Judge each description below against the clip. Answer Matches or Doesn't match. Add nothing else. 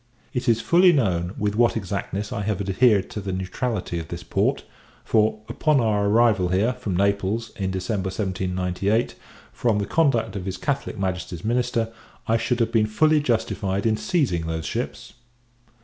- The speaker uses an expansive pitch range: Doesn't match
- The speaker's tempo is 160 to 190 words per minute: Matches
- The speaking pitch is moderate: Doesn't match